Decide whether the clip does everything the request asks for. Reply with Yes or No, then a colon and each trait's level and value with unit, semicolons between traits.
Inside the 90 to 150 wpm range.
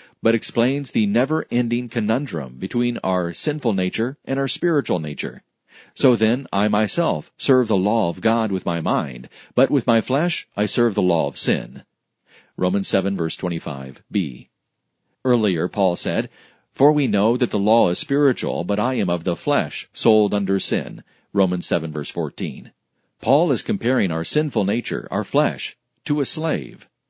No: average, 165 wpm